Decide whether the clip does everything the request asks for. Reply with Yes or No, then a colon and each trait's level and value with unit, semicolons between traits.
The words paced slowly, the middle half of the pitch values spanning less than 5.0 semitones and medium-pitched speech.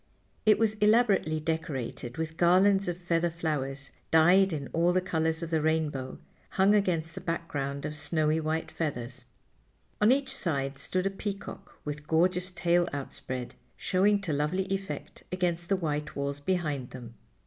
No: average, 155 wpm; average, 3.8 semitones; medium, 165 Hz